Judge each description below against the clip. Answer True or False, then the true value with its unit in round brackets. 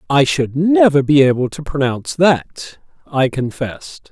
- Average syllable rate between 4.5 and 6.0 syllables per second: False (4.3 syllables/s)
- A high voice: False (145 Hz)